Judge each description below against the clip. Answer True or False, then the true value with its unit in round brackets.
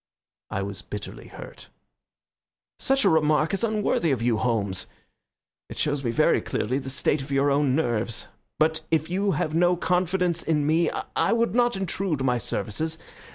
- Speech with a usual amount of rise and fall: False (6.0 semitones)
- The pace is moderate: True (165 wpm)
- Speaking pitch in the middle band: True (155 Hz)